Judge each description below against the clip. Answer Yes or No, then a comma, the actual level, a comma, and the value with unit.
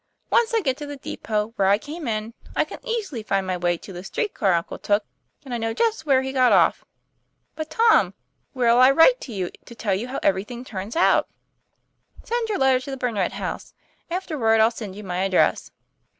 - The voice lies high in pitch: Yes, high, 240 Hz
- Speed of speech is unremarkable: No, fast, 220 wpm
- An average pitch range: No, wide, 6.5 semitones